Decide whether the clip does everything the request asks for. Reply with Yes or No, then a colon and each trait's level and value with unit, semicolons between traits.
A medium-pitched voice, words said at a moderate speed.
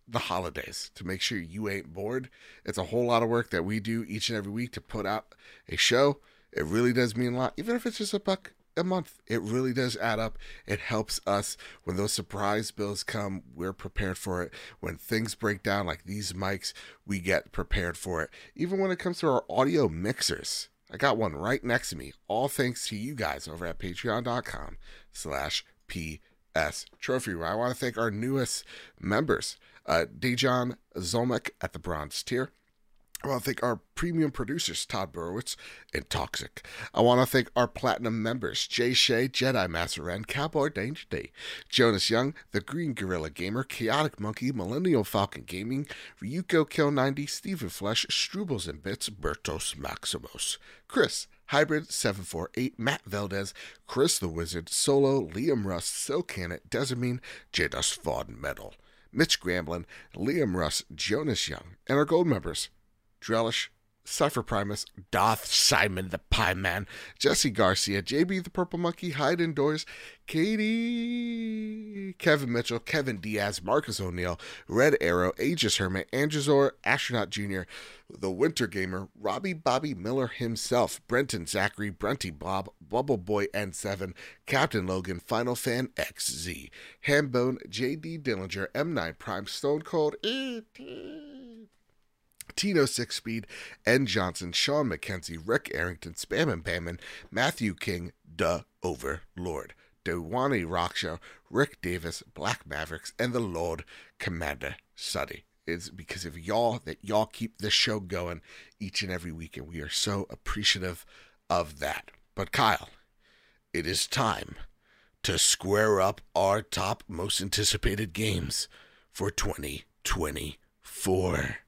No: low, 110 Hz; average, 150 wpm